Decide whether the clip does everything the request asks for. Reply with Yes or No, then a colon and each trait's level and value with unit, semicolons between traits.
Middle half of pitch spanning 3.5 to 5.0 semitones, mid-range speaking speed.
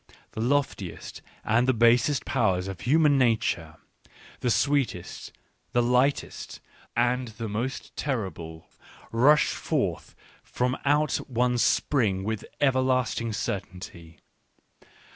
No: average, 4.4 semitones; slow, 105 wpm